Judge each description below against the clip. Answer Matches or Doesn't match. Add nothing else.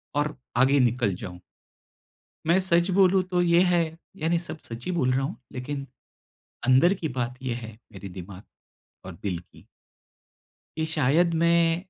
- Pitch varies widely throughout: Matches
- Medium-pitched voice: Matches